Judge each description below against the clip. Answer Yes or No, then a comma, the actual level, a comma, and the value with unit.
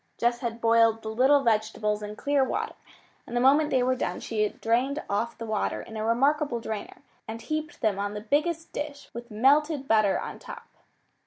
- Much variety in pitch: No, average, 4.3 semitones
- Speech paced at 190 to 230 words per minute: Yes, average, 195 wpm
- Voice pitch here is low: No, high, 235 Hz